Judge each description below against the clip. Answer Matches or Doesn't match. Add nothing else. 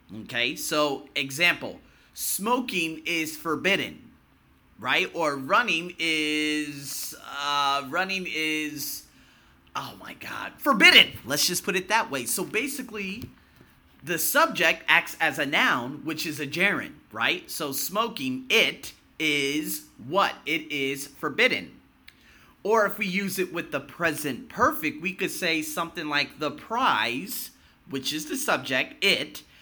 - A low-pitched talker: Doesn't match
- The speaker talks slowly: Matches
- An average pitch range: Matches